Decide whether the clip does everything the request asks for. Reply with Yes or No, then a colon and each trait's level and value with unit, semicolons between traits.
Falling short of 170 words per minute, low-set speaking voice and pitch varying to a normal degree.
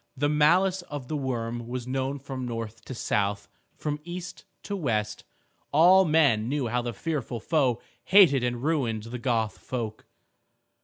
Yes: average, 155 wpm; low, 130 Hz; average, 4.6 semitones